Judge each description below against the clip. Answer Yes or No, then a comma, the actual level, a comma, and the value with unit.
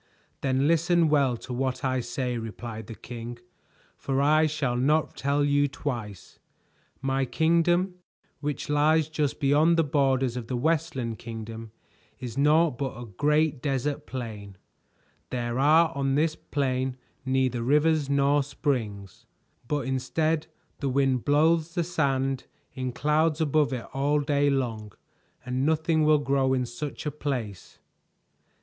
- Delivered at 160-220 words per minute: No, average, 140 wpm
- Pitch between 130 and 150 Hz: Yes, medium, 140 Hz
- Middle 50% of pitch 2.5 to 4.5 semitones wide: Yes, average, 3.3 semitones